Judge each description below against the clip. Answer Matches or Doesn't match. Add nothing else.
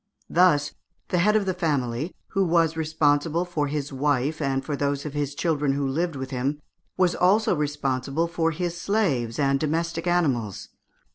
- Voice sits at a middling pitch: Matches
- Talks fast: Doesn't match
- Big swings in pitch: Doesn't match